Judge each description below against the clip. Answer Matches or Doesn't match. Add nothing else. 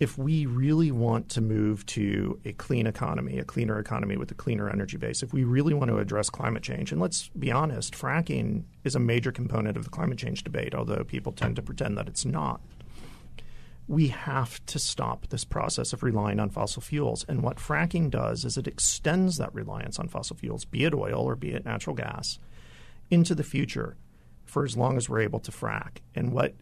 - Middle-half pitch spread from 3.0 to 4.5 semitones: Doesn't match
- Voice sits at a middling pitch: Doesn't match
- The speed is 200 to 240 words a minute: Matches